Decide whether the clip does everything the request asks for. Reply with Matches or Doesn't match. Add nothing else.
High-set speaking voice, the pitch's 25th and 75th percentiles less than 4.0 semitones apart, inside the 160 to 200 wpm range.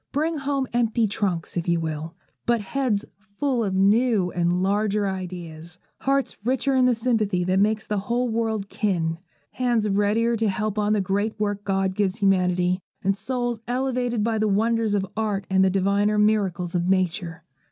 Matches